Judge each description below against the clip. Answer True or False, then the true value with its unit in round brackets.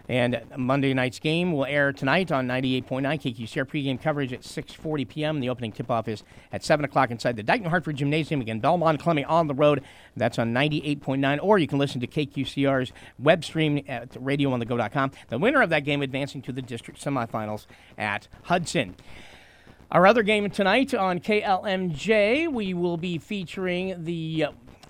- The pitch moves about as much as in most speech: True (4.6 semitones)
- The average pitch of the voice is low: False (145 Hz)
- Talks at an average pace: True (180 wpm)